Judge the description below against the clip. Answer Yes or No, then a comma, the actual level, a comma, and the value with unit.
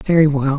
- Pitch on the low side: No, medium, 145 Hz